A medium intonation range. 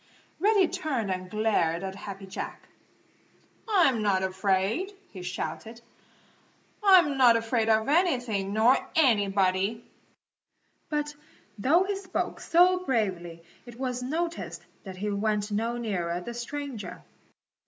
No: wide, 7.0 semitones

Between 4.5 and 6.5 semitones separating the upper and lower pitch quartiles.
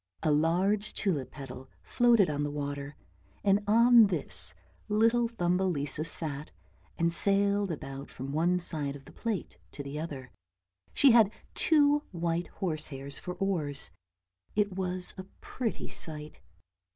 Yes: wide, 5.6 semitones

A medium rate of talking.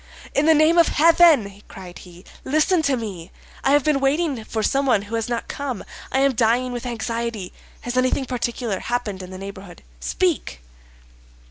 Yes: average, 170 wpm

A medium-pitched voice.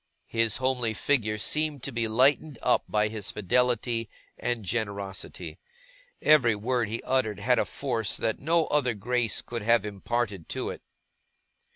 No: low, 115 Hz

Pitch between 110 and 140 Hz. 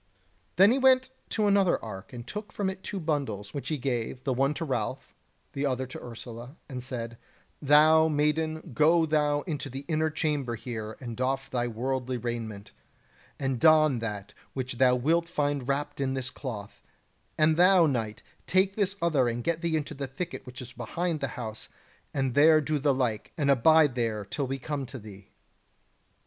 Yes: low, 135 Hz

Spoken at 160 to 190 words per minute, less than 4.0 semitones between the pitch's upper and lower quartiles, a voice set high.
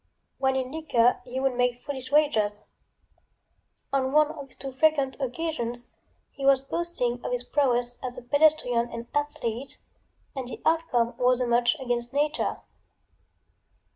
No: average, 145 wpm; average, 3.1 semitones; very high, 260 Hz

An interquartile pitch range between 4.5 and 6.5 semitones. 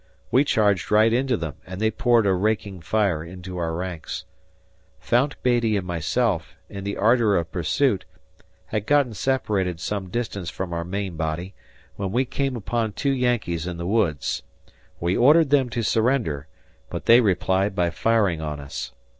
Yes: average, 5.2 semitones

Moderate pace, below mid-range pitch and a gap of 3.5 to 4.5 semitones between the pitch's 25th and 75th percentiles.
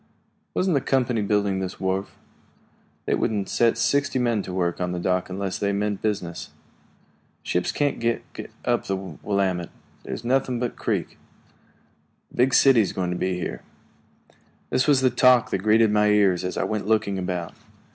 Yes: average, 175 wpm; low, 105 Hz; average, 4.2 semitones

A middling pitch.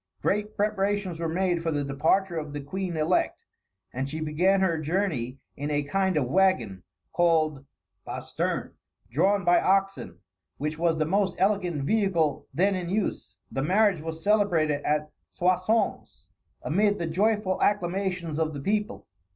Yes: medium, 175 Hz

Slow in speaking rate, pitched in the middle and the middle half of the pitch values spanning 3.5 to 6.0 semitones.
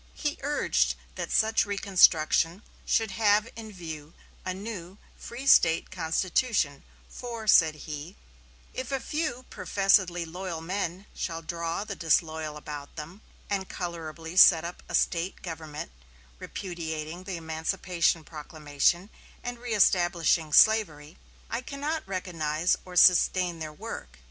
Yes: slow, 125 wpm; medium, 175 Hz; average, 4.2 semitones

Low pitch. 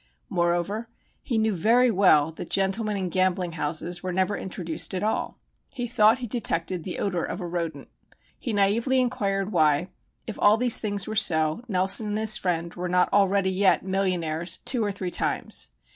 No: high, 190 Hz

